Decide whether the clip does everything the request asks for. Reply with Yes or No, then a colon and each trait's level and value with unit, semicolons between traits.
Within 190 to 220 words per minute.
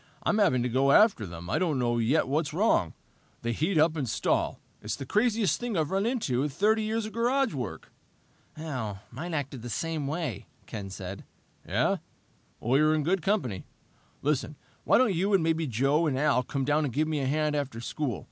Yes: fast, 205 wpm